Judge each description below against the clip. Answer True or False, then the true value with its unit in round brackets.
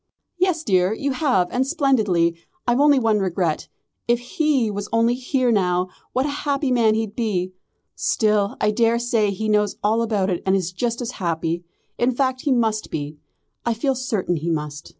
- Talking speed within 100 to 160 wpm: False (180 wpm)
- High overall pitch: True (220 Hz)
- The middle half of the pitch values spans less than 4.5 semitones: False (5.2 semitones)